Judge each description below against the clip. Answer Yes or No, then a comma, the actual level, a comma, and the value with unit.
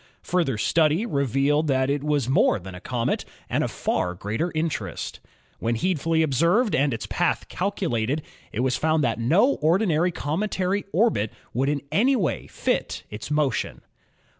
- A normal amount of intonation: No, wide, 5.7 semitones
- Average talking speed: Yes, average, 165 wpm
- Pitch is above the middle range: No, medium, 150 Hz